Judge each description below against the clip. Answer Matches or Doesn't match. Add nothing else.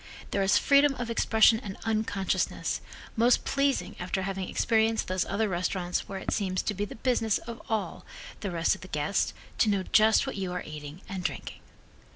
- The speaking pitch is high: Matches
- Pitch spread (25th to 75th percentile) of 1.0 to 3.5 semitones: Matches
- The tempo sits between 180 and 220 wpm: Matches